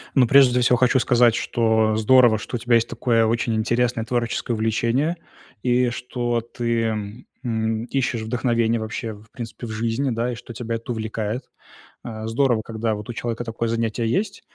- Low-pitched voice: Yes, low, 115 Hz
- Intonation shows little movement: Yes, narrow, 1.7 semitones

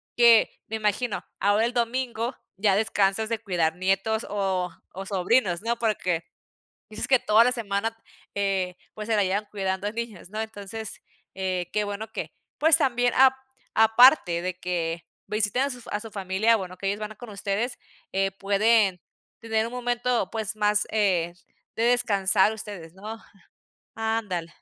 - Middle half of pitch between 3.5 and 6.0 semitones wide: No, average, 3.0 semitones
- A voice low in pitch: No, high, 210 Hz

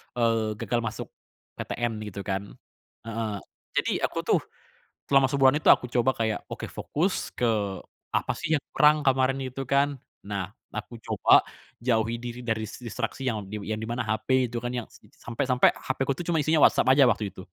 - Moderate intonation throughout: Yes, average, 3.3 semitones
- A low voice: Yes, low, 120 Hz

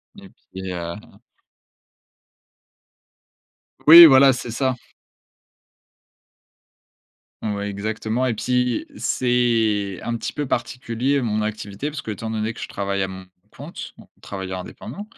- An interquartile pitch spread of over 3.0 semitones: Yes, average, 4.1 semitones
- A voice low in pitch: Yes, low, 110 Hz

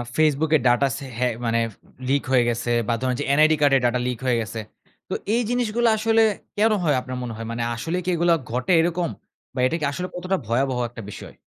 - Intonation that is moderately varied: No, wide, 6.2 semitones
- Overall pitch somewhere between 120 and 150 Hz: Yes, medium, 140 Hz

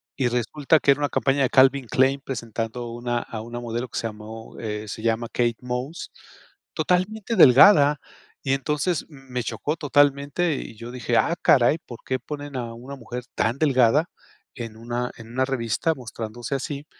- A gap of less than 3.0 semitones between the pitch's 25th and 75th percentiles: No, average, 3.5 semitones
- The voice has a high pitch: No, low, 125 Hz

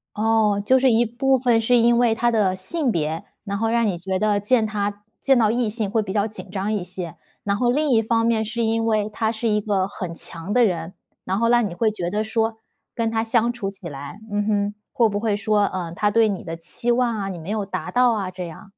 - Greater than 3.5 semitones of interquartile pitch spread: No, average, 2.8 semitones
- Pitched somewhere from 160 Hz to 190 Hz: No, high, 215 Hz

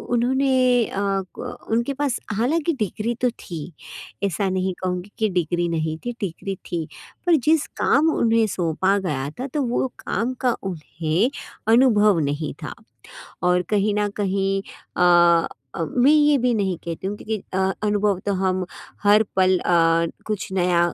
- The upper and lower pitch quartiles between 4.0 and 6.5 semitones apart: Yes, average, 4.7 semitones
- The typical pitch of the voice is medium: No, high, 195 Hz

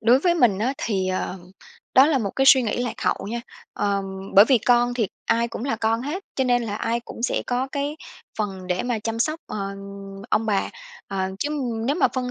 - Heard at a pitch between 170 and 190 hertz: No, high, 235 Hz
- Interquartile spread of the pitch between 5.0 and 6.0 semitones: No, average, 3.8 semitones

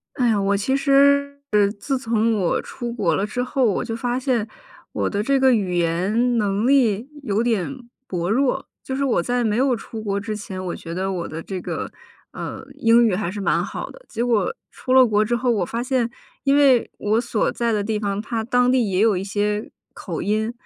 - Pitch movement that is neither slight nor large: Yes, average, 3.6 semitones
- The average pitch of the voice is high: Yes, high, 225 Hz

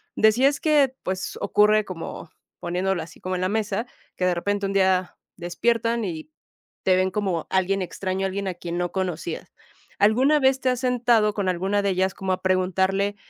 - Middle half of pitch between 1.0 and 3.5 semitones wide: Yes, average, 2.8 semitones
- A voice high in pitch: Yes, high, 195 Hz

